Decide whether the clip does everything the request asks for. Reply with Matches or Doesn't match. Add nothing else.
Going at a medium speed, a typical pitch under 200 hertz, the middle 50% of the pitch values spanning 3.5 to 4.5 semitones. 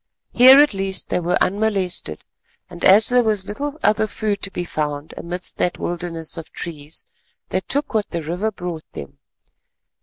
Matches